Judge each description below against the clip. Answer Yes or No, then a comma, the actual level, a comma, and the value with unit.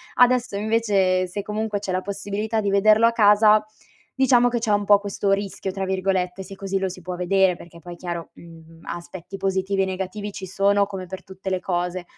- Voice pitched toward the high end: Yes, high, 195 Hz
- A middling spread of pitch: No, narrow, 2.0 semitones